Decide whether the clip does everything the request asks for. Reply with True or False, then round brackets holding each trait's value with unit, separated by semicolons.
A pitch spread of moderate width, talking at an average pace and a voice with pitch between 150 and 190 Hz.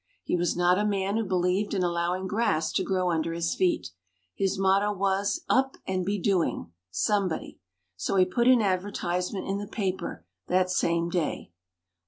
False (2.2 semitones; 170 wpm; 185 Hz)